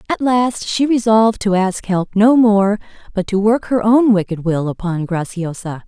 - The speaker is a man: No, female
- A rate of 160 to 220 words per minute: Yes, average, 185 wpm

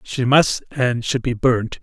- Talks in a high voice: No, low, 125 Hz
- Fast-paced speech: No, average, 195 wpm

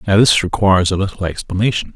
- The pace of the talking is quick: No, average, 185 wpm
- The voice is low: Yes, very low, 95 Hz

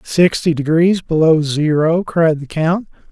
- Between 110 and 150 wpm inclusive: Yes, slow, 135 wpm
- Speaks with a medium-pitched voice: Yes, medium, 160 Hz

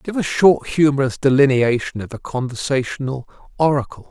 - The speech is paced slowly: Yes, slow, 130 wpm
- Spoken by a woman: No, male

